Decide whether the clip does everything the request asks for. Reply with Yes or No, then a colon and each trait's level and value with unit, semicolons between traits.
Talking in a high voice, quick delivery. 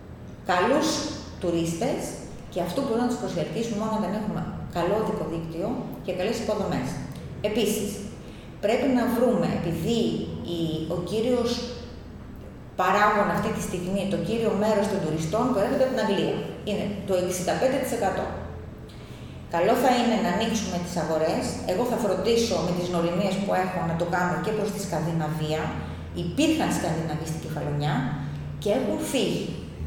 No: high, 200 Hz; average, 145 wpm